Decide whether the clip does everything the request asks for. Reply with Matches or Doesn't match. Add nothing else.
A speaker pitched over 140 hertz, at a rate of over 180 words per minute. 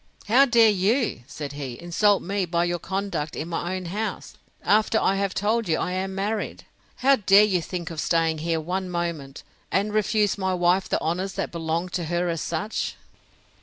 Matches